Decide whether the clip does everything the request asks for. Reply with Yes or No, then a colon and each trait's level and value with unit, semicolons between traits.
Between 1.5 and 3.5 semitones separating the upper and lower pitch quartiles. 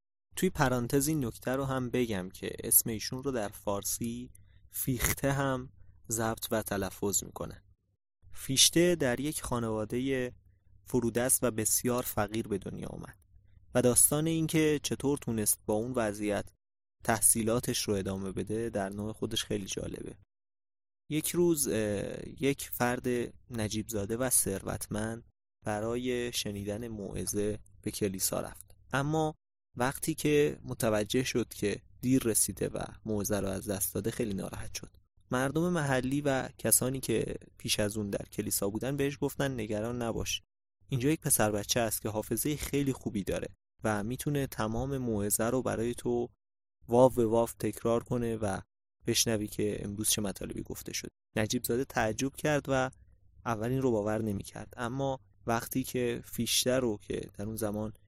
No: average, 3.9 semitones